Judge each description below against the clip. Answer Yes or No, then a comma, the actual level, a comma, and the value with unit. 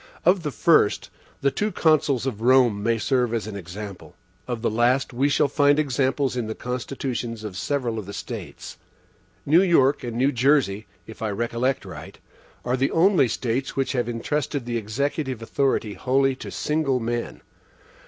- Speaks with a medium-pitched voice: No, low, 125 Hz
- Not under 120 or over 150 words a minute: No, average, 170 wpm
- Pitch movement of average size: Yes, average, 3.4 semitones